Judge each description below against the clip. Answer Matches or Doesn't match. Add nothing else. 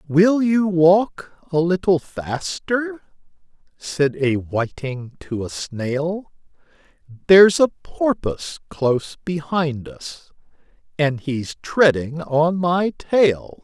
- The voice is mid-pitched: Matches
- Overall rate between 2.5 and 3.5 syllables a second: Matches